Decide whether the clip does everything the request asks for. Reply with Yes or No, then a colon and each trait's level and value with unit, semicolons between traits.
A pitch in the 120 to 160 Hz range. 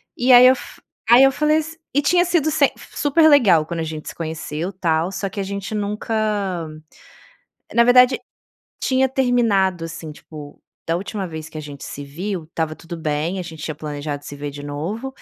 No: medium, 185 Hz